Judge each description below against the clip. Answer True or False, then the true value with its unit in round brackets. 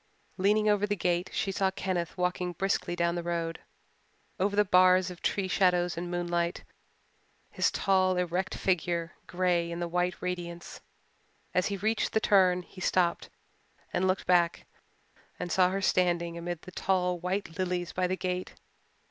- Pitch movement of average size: False (1.4 semitones)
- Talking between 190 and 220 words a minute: False (160 wpm)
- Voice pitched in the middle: True (180 Hz)